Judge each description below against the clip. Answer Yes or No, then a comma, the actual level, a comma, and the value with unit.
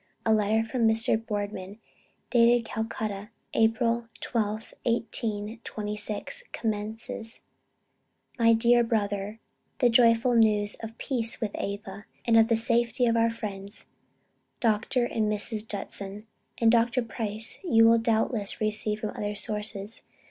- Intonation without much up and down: Yes, narrow, 1.7 semitones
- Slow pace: Yes, slow, 125 wpm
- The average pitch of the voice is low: No, high, 225 Hz